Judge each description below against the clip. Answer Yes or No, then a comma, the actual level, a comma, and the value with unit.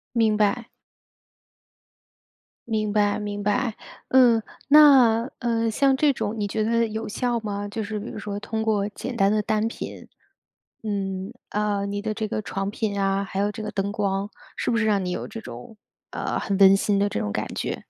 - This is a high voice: Yes, high, 210 Hz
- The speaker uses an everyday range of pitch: No, narrow, 2.1 semitones